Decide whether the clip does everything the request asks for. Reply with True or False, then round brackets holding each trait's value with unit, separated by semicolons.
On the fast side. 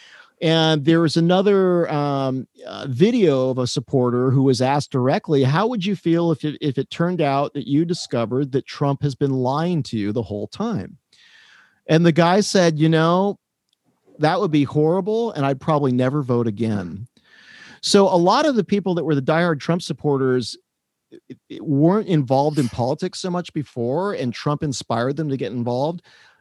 False (185 wpm)